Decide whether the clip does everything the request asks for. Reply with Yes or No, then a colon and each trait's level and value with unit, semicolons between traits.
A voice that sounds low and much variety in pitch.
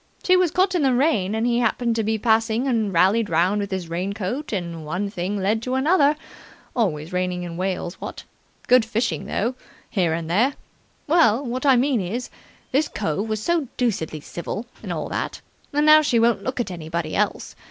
No: high, 220 Hz; wide, 5.9 semitones